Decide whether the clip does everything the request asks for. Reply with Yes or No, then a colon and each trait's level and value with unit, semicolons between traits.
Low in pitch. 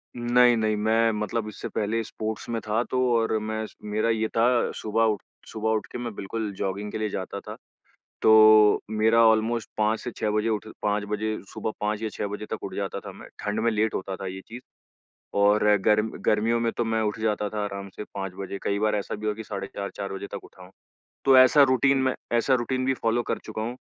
Yes: low, 110 Hz